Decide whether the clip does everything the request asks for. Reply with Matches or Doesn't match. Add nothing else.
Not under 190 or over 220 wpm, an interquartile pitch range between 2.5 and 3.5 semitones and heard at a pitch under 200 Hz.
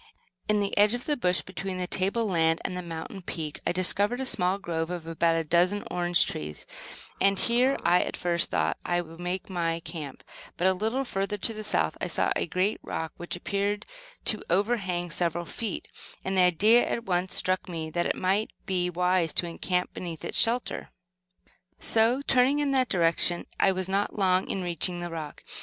Matches